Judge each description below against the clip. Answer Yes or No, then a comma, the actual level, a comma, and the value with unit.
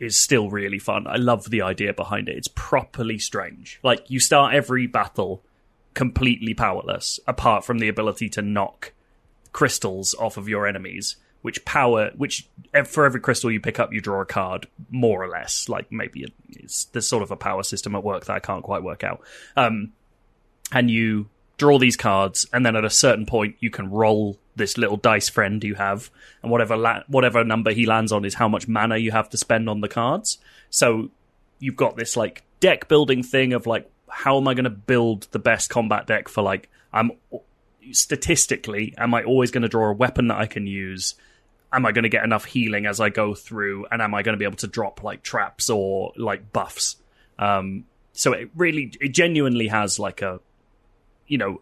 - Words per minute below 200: No, fast, 205 wpm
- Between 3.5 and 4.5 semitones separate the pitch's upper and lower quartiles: No, average, 3.0 semitones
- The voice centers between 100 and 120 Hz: Yes, low, 110 Hz